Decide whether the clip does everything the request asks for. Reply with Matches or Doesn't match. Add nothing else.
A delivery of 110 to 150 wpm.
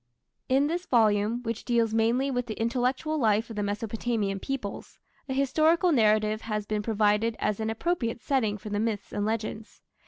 Doesn't match